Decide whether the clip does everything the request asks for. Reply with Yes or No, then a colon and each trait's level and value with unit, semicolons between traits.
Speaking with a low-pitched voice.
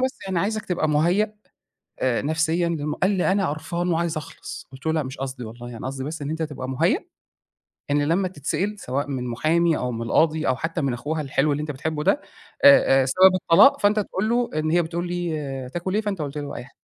No: medium, 160 Hz